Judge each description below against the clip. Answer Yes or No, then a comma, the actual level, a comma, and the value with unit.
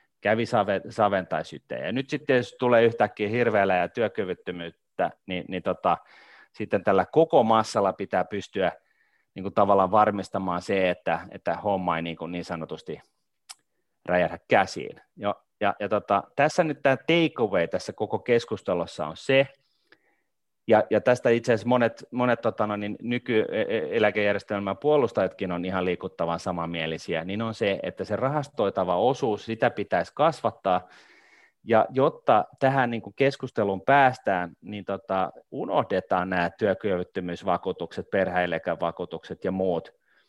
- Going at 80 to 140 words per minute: Yes, average, 130 wpm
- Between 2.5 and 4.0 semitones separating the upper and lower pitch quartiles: No, average, 4.7 semitones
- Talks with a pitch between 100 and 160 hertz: Yes, low, 105 Hz